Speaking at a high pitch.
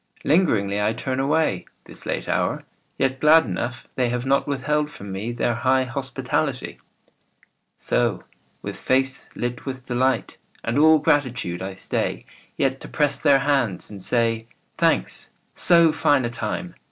No: low, 130 Hz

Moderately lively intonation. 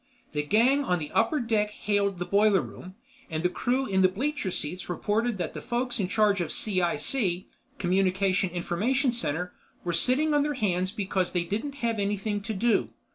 Yes: average, 4.7 semitones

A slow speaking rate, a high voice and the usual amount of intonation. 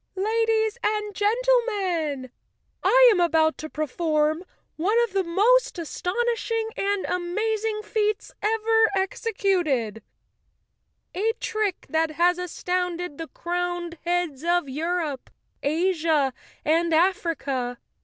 Yes: slow, 105 wpm; very high, 355 Hz; average, 4.9 semitones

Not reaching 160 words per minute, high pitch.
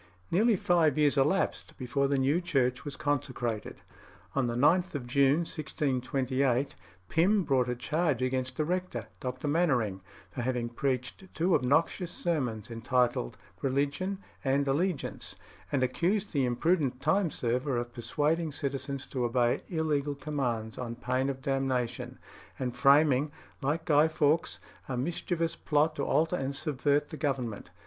No: average, 140 wpm; medium, 140 Hz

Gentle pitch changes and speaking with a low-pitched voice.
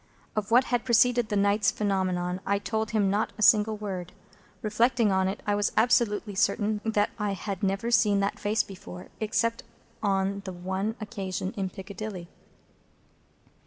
No: narrow, 2.1 semitones; high, 205 Hz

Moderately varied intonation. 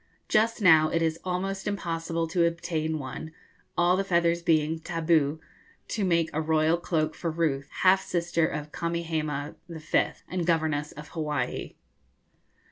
No: narrow, 1.7 semitones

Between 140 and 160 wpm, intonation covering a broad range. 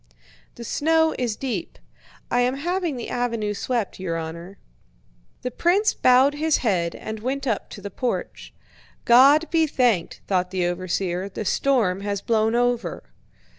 Yes: average, 150 wpm; wide, 6.1 semitones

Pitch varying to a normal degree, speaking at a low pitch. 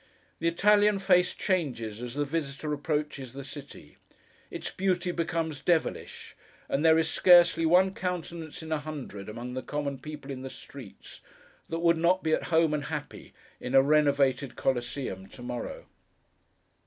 No: average, 3.8 semitones; medium, 150 Hz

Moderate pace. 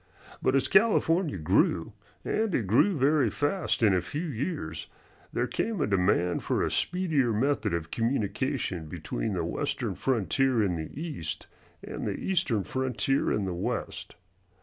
Yes: average, 150 wpm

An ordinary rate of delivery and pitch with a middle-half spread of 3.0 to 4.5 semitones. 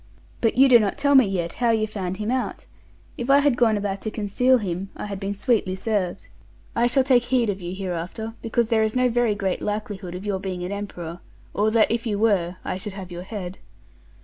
No: fast, 230 wpm; average, 3.6 semitones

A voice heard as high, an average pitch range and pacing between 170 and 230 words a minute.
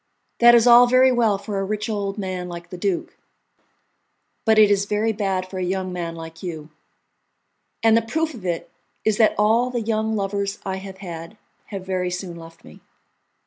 Yes: high, 200 Hz; average, 3.3 semitones; average, 190 wpm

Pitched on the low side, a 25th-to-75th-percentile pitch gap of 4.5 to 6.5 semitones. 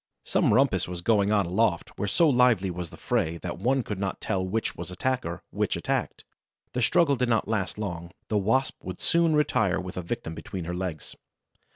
Yes: low, 100 Hz; average, 5.3 semitones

